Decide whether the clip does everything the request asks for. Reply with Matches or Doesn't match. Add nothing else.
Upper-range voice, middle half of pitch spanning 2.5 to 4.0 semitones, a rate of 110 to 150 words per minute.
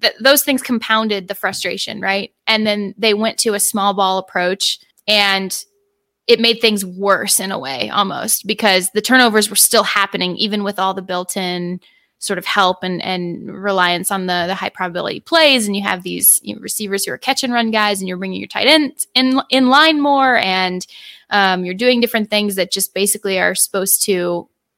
Doesn't match